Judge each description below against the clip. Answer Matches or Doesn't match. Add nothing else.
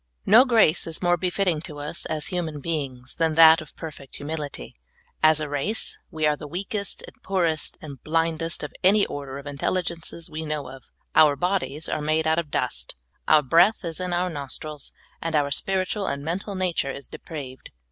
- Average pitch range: Matches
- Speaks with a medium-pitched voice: Matches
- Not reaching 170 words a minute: Doesn't match